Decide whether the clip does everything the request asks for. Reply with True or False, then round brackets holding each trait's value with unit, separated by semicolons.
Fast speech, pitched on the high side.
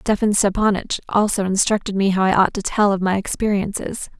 False (185 wpm; 200 Hz)